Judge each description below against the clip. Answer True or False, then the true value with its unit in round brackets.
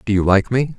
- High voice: False (110 Hz)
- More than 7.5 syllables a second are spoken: False (5.8 syllables/s)